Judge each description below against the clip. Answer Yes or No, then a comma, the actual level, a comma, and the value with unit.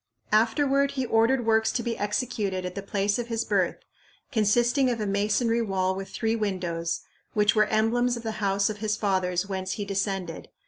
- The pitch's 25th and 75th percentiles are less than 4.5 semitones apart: Yes, average, 2.9 semitones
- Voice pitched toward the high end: Yes, high, 210 Hz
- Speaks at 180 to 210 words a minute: Yes, average, 185 wpm